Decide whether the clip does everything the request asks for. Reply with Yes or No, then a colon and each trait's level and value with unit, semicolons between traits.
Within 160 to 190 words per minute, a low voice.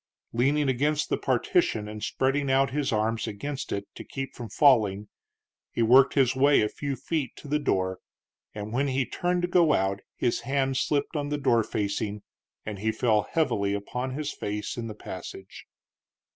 Yes: average, 180 wpm; low, 125 Hz